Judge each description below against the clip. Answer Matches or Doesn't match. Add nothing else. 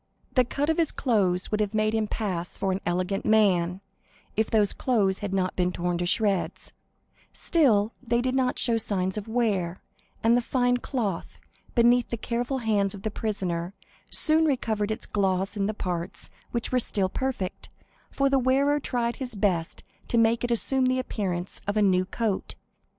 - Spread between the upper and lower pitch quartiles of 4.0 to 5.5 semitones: Matches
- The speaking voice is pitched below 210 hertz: Doesn't match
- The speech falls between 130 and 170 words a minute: Doesn't match